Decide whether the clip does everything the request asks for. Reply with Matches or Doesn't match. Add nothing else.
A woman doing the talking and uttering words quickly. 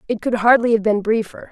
Matches